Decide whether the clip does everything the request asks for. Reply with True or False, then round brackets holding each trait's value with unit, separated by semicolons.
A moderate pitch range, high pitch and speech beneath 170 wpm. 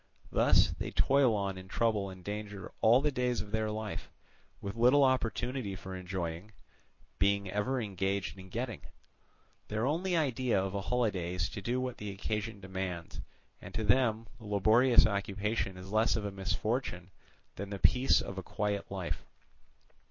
False (3.6 semitones; 105 Hz; 160 wpm)